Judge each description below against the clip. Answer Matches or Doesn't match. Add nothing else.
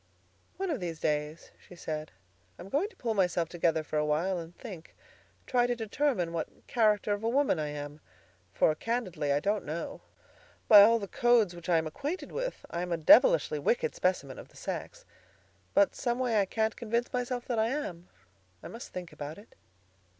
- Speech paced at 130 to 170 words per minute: Doesn't match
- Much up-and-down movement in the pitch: Matches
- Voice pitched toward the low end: Doesn't match